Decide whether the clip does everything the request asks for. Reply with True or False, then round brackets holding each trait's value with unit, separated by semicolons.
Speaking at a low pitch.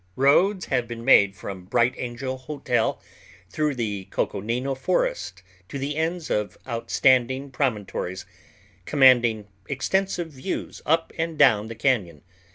True (130 Hz)